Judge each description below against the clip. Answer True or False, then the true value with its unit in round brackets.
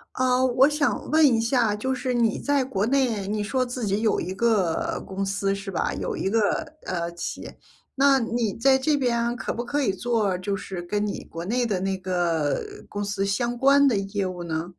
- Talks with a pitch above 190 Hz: True (220 Hz)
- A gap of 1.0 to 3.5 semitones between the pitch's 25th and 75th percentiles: False (4.7 semitones)